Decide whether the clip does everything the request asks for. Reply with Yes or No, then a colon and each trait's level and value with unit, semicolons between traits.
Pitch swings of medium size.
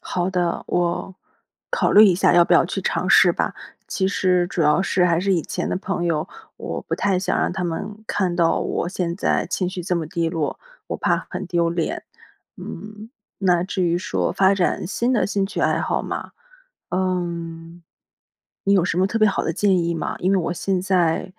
No: narrow, 2.2 semitones